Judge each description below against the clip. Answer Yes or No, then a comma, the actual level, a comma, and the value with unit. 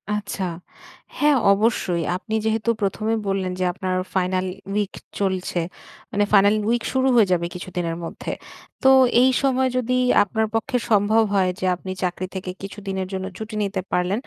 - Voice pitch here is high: Yes, high, 200 Hz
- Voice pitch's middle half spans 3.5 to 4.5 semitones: No, average, 3.1 semitones